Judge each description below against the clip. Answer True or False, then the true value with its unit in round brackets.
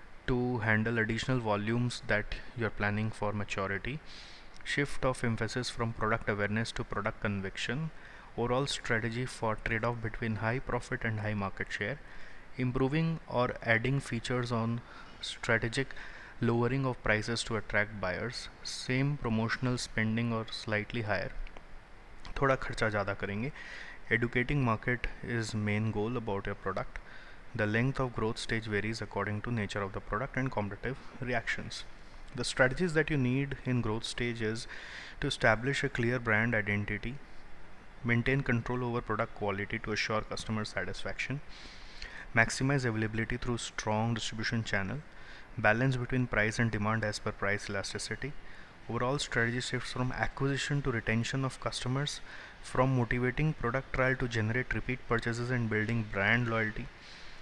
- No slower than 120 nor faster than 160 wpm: True (140 wpm)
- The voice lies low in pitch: True (115 Hz)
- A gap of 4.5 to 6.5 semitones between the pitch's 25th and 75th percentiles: False (2.9 semitones)